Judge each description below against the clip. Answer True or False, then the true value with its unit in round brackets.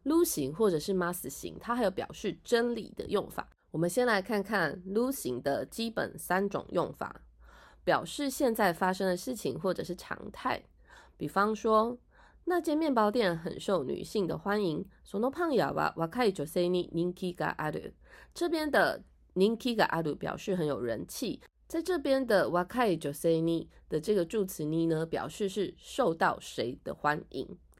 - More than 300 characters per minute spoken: False (240 characters per minute)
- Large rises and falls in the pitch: True (6.0 semitones)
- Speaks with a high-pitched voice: True (195 Hz)